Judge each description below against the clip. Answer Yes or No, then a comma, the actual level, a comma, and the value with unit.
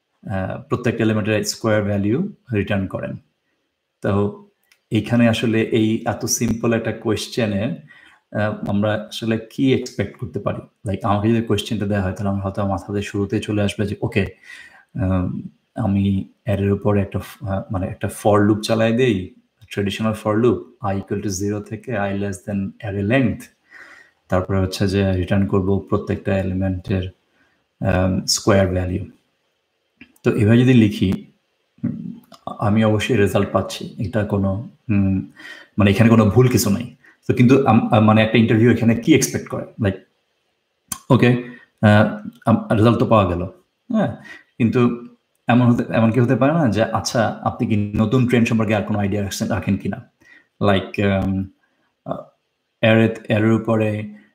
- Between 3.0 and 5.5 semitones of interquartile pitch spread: No, narrow, 2.4 semitones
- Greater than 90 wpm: Yes, average, 115 wpm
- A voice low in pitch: Yes, low, 105 Hz